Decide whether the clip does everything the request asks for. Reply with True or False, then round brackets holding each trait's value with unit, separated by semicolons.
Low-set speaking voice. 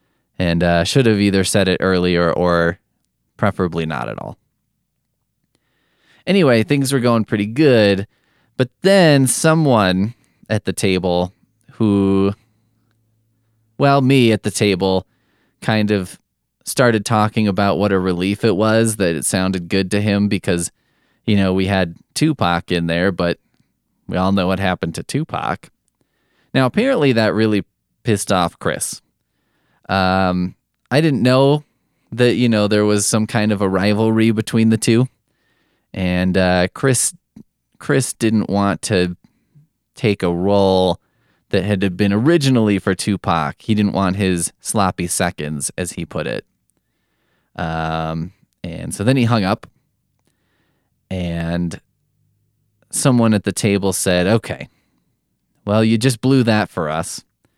True (105 Hz)